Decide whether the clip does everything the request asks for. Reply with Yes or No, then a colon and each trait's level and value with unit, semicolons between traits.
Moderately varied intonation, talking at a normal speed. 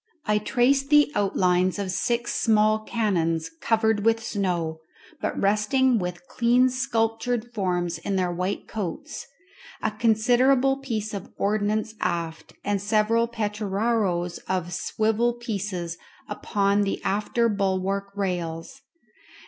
No: average, 3.8 semitones; slow, 115 wpm